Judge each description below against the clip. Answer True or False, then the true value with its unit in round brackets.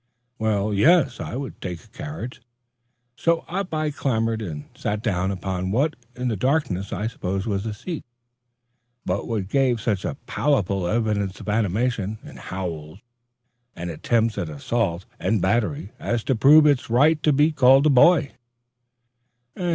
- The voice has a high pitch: False (110 Hz)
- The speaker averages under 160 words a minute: True (150 wpm)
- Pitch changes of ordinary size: False (6.1 semitones)